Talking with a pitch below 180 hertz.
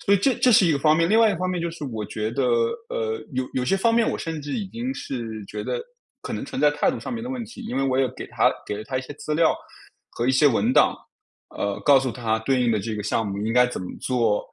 Yes: medium, 140 Hz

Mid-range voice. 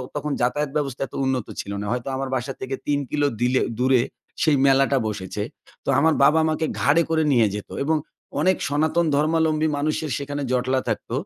Yes: medium, 145 Hz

